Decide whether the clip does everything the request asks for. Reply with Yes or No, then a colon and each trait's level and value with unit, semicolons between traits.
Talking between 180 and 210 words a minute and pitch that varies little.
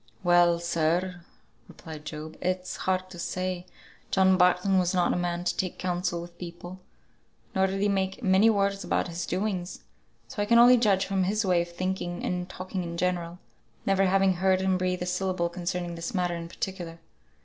Yes: average, 185 wpm; narrow, 1.6 semitones